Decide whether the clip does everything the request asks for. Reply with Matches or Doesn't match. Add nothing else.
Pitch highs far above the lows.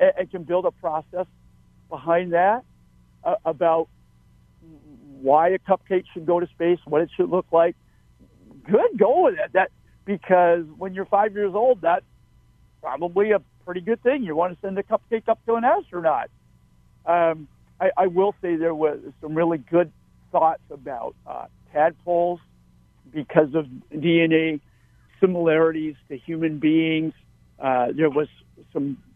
Doesn't match